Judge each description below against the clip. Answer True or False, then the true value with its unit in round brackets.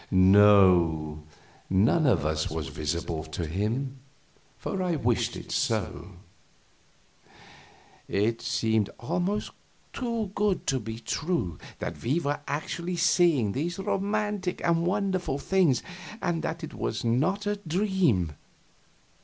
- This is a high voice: False (135 Hz)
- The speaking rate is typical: False (120 wpm)